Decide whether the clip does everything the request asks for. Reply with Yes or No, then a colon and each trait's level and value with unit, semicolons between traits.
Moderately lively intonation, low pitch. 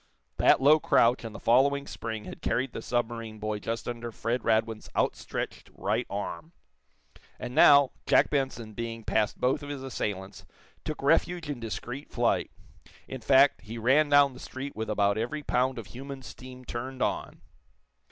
Yes: average, 3.5 semitones; low, 125 Hz